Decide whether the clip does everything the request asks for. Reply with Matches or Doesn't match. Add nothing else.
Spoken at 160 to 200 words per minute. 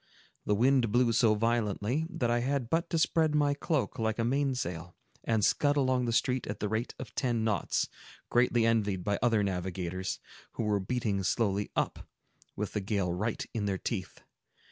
Matches